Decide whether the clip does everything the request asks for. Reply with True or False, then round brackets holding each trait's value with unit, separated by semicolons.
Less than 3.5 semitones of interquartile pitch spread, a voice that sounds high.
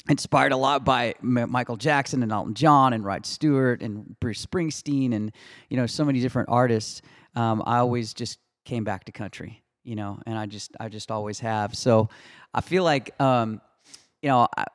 False (3.0 semitones; 120 Hz)